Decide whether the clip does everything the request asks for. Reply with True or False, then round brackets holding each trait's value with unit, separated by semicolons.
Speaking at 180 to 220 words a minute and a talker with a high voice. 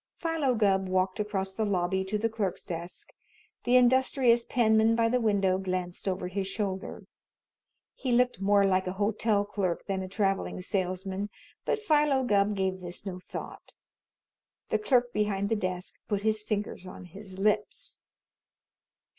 False (155 wpm; 200 Hz)